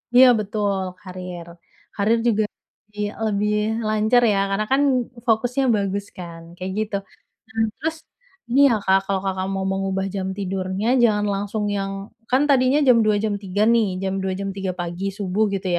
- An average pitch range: No, narrow, 2.2 semitones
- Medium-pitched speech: No, high, 200 Hz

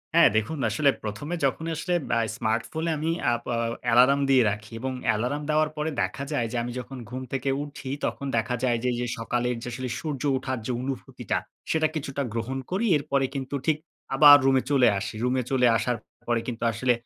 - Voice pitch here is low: Yes, low, 130 Hz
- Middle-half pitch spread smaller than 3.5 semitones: Yes, average, 3.0 semitones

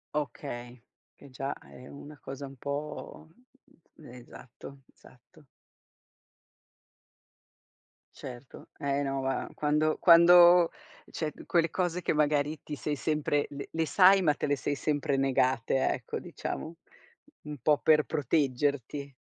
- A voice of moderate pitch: Yes, medium, 145 Hz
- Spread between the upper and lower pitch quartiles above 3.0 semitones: No, narrow, 2.4 semitones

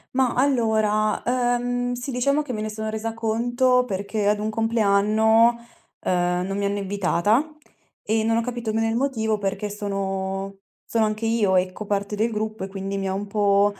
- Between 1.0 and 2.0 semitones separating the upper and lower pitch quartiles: No, narrow, 2.6 semitones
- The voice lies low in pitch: No, high, 215 Hz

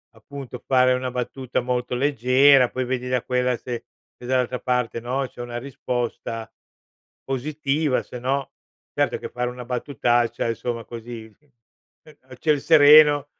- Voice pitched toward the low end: Yes, low, 125 Hz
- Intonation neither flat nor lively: No, narrow, 2.1 semitones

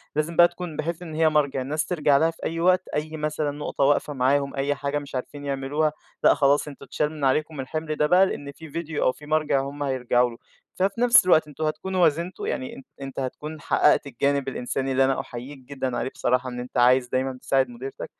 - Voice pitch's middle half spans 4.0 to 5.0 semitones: No, average, 2.8 semitones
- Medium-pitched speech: Yes, medium, 145 Hz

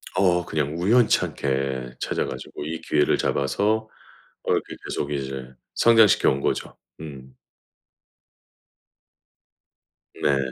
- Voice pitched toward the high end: No, very low, 75 Hz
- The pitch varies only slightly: No, average, 5.3 semitones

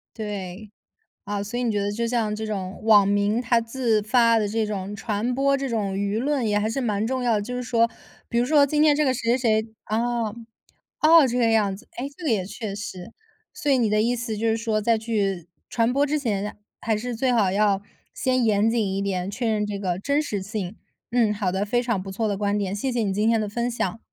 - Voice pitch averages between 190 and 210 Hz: No, high, 220 Hz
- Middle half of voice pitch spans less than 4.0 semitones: Yes, average, 2.9 semitones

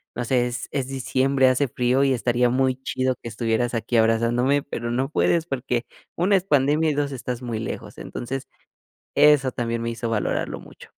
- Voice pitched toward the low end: Yes, low, 125 Hz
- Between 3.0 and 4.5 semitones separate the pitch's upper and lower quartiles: No, narrow, 2.4 semitones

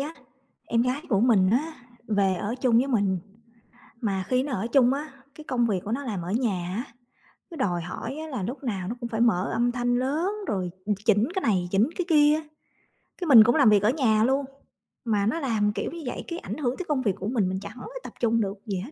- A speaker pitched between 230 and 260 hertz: Yes, high, 235 Hz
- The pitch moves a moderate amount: Yes, average, 5.0 semitones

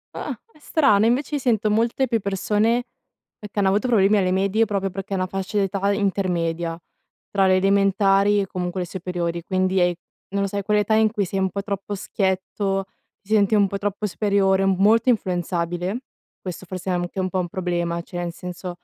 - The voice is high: Yes, high, 195 Hz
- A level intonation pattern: Yes, narrow, 2.0 semitones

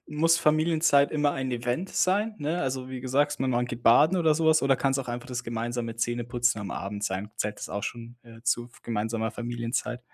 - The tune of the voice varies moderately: Yes, average, 3.8 semitones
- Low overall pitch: Yes, low, 125 Hz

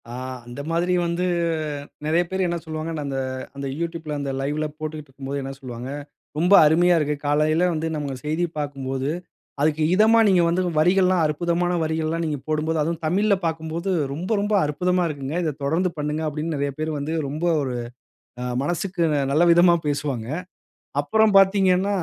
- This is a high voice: No, medium, 160 Hz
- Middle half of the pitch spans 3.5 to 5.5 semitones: No, average, 3.1 semitones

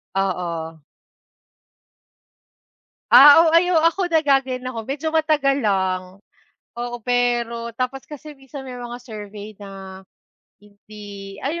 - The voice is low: No, high, 240 Hz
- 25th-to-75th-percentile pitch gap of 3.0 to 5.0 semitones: No, wide, 5.6 semitones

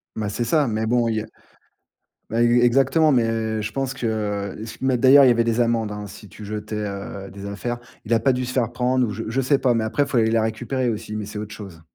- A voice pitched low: Yes, low, 115 Hz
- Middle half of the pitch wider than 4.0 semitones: No, narrow, 2.6 semitones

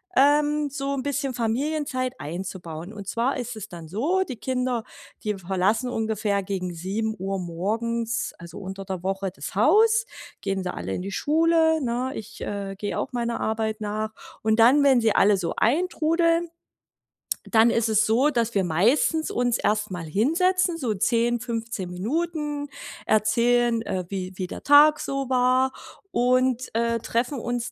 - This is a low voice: No, high, 230 Hz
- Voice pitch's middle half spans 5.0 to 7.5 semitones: Yes, average, 5.3 semitones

